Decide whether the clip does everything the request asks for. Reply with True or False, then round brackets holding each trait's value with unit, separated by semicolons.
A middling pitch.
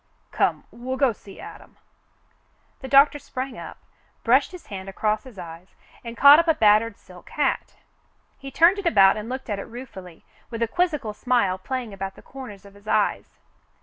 False (230 Hz)